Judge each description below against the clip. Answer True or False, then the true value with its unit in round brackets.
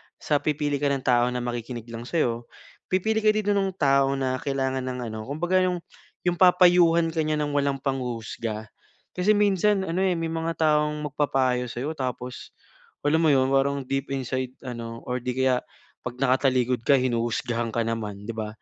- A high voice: False (135 Hz)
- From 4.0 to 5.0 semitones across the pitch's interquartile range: True (4.7 semitones)